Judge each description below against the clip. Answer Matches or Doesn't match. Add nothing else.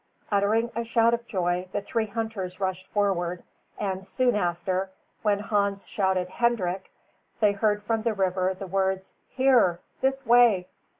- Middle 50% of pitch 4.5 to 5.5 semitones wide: Doesn't match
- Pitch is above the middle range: Matches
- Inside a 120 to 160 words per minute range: Matches